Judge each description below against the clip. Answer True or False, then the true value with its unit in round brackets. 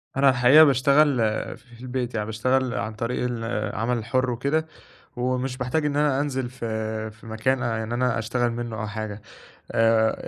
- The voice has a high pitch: False (120 Hz)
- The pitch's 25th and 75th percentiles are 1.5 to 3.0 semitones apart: True (2.7 semitones)